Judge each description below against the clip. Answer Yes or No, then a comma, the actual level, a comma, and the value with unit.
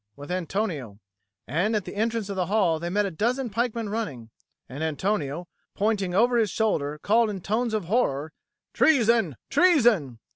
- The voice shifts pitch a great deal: Yes, wide, 6.0 semitones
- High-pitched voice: Yes, high, 205 Hz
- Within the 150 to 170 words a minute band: Yes, average, 160 wpm